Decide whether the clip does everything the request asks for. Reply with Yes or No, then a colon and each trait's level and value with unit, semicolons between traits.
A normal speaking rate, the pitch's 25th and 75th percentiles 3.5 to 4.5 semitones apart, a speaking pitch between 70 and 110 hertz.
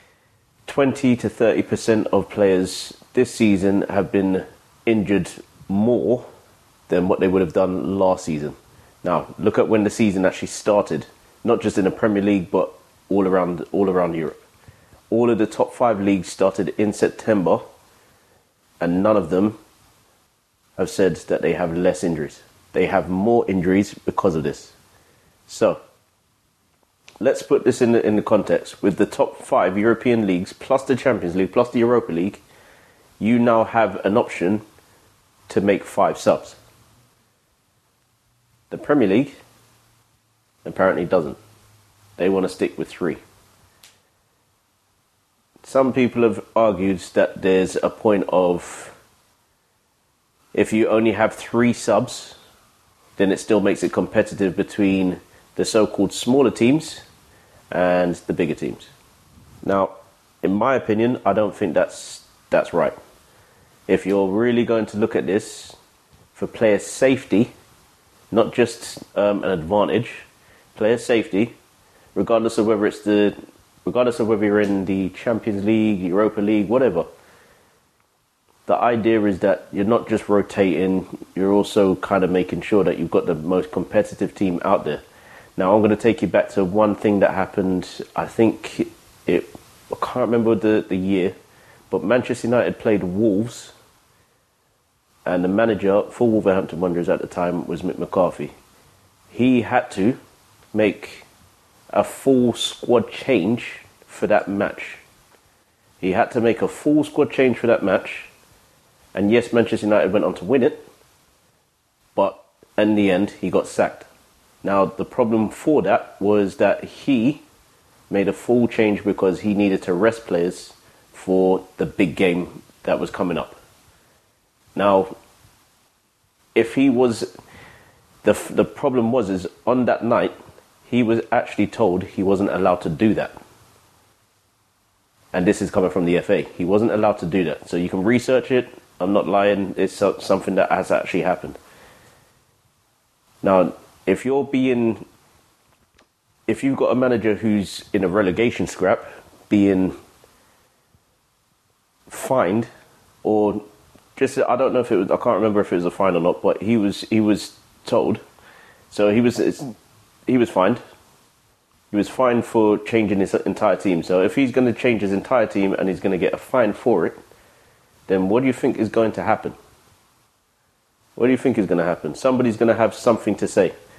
No: average, 155 wpm; average, 3.1 semitones; low, 105 Hz